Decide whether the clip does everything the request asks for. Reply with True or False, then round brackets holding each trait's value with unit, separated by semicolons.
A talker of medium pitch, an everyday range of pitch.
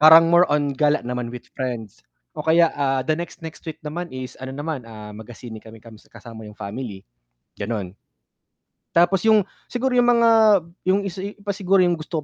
False (150 Hz; 7.1 semitones)